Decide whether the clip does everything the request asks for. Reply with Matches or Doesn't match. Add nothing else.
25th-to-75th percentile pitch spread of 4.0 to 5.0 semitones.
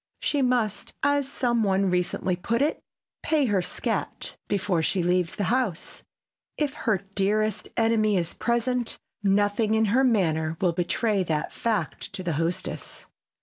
Matches